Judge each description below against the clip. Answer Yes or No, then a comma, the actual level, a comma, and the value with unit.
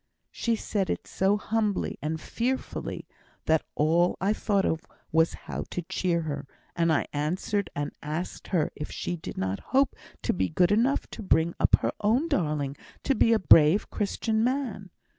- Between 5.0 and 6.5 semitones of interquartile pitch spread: Yes, wide, 5.5 semitones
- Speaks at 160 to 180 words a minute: Yes, average, 175 wpm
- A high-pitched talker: No, medium, 180 Hz